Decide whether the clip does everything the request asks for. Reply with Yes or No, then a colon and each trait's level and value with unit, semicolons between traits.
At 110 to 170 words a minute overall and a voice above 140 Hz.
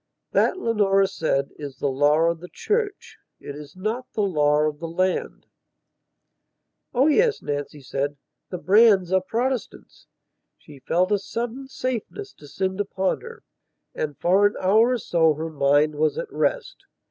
Yes: average, 155 wpm; medium, 185 Hz